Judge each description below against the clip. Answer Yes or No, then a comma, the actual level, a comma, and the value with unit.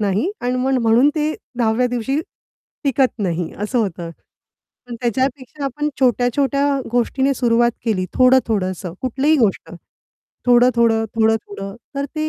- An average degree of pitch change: Yes, average, 3.3 semitones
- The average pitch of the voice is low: No, high, 245 Hz